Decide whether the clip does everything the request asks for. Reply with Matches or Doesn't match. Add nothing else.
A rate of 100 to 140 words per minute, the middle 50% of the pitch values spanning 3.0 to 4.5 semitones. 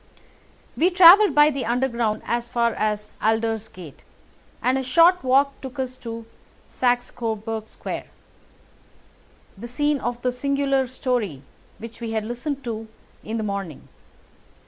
Matches